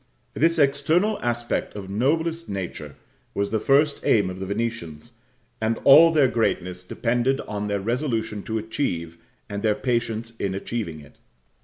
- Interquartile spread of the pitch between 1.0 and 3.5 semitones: No, average, 5.3 semitones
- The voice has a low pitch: Yes, low, 115 Hz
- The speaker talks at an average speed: Yes, average, 150 wpm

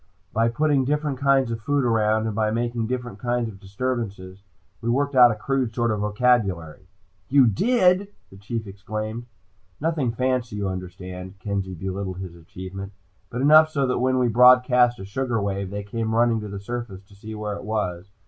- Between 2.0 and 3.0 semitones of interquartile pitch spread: No, average, 4.2 semitones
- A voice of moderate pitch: No, low, 115 Hz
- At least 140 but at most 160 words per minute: No, average, 185 wpm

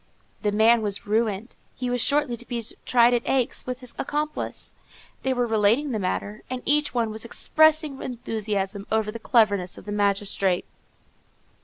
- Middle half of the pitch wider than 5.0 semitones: No, average, 3.4 semitones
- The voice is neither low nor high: No, high, 230 Hz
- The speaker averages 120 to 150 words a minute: No, average, 165 wpm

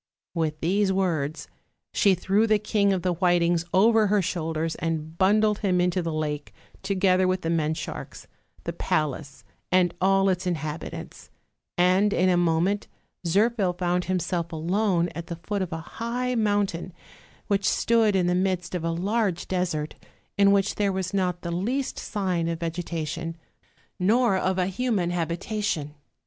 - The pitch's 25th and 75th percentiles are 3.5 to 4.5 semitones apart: No, average, 3.1 semitones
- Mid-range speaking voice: Yes, medium, 180 Hz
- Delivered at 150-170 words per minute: Yes, average, 160 wpm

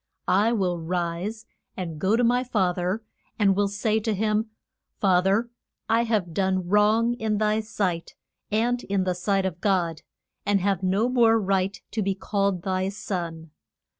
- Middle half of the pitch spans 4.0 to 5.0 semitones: No, average, 2.9 semitones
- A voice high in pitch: Yes, high, 200 Hz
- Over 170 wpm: No, average, 165 wpm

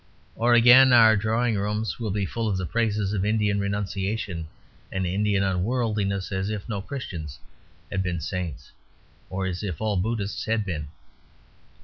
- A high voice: No, low, 100 Hz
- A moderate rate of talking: Yes, average, 155 wpm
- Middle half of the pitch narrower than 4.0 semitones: Yes, average, 2.7 semitones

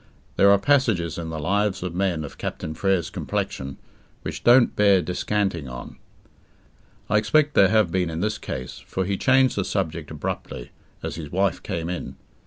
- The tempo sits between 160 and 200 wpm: Yes, average, 175 wpm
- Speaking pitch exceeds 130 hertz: No, very low, 95 Hz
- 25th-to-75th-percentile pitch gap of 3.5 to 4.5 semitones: Yes, average, 4.0 semitones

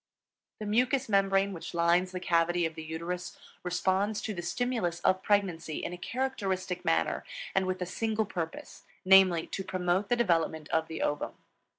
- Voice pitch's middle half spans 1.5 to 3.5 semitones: Yes, average, 2.9 semitones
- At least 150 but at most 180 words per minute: Yes, average, 170 wpm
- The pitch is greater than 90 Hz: Yes, medium, 185 Hz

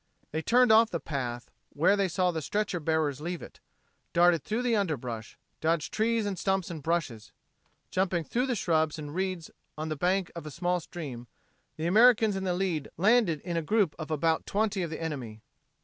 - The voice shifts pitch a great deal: No, average, 4.1 semitones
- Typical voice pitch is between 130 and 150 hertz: No, medium, 170 Hz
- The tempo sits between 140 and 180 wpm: No, average, 195 wpm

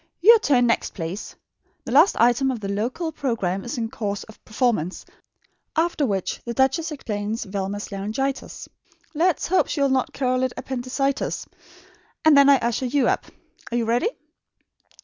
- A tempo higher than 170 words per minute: No, average, 165 wpm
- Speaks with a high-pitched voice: Yes, high, 245 Hz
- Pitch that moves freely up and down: No, average, 4.6 semitones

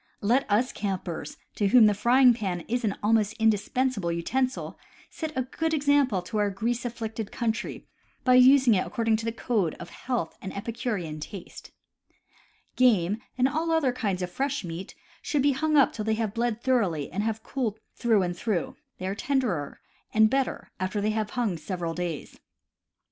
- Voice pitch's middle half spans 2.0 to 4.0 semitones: No, average, 4.6 semitones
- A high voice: Yes, high, 220 Hz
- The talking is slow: No, average, 180 wpm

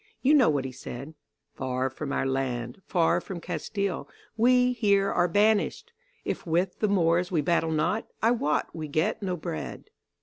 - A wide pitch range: Yes, wide, 5.8 semitones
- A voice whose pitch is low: No, medium, 170 Hz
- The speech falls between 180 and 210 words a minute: No, average, 170 wpm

